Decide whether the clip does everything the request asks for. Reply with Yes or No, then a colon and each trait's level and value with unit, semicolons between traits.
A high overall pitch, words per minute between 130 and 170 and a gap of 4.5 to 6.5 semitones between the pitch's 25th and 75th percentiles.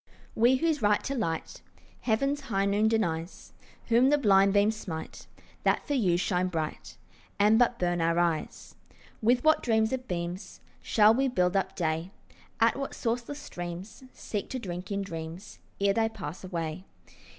Yes: high, 200 Hz; average, 160 wpm; average, 5.1 semitones